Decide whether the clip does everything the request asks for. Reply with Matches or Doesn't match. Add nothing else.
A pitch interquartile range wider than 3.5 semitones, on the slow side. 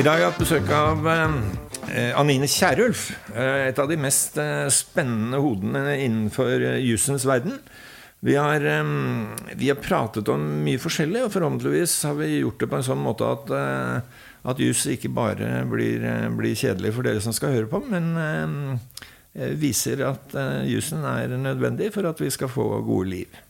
Doesn't match